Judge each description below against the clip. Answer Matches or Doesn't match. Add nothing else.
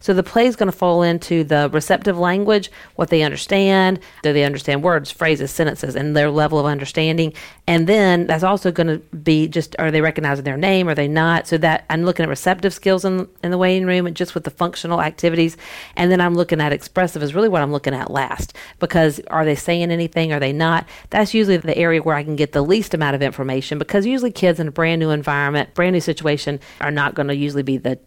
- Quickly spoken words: Matches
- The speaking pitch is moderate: Matches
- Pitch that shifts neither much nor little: Matches